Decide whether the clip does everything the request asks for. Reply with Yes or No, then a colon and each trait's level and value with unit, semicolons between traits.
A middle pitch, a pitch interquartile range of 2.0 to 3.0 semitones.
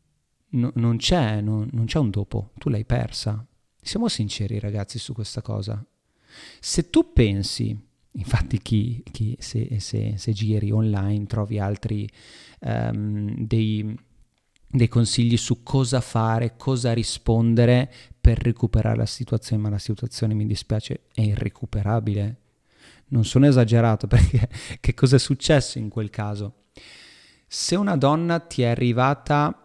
No: low, 115 Hz; narrow, 2.6 semitones